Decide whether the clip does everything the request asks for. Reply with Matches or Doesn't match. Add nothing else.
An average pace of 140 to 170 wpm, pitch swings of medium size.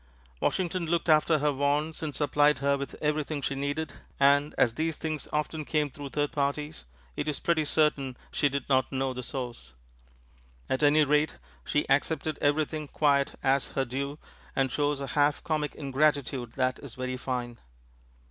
Doesn't match